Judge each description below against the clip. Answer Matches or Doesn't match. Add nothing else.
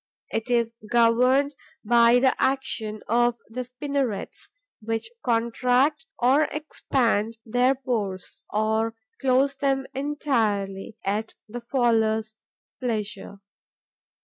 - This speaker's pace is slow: Matches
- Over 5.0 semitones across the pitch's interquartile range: Doesn't match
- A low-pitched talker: Doesn't match